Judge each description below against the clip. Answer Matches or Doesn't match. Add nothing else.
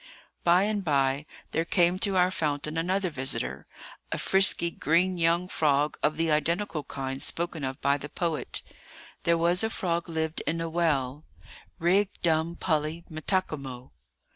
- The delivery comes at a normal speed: Matches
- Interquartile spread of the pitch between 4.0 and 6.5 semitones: Doesn't match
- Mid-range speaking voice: Matches